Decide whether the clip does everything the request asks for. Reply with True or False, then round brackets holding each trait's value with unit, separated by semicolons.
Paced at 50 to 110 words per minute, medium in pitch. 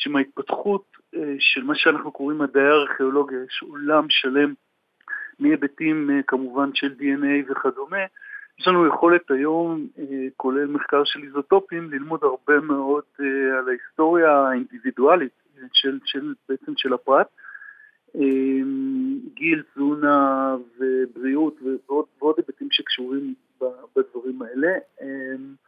True (100 wpm; 145 Hz)